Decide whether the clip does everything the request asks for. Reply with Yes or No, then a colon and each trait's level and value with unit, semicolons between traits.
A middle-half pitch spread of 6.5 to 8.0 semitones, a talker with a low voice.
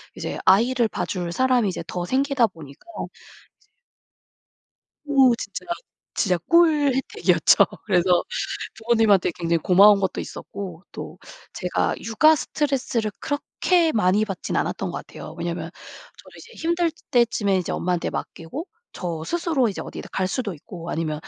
No: wide, 6.8 semitones; high, 215 Hz